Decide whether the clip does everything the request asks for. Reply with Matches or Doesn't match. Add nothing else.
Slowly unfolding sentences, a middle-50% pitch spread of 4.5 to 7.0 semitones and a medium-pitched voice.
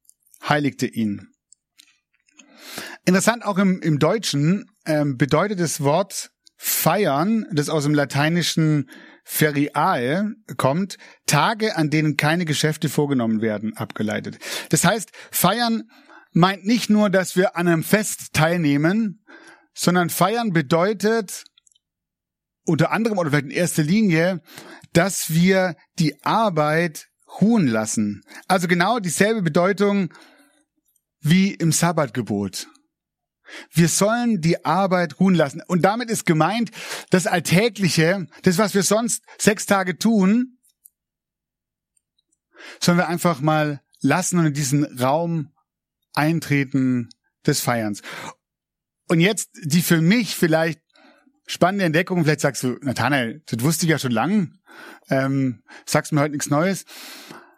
Matches